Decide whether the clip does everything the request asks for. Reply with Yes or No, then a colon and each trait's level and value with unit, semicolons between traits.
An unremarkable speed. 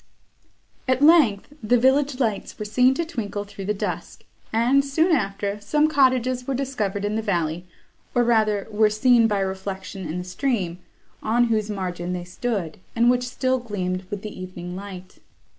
Yes: average, 170 wpm